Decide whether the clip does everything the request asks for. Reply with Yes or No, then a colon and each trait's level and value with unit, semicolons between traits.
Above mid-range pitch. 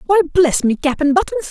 Yes: very high, 320 Hz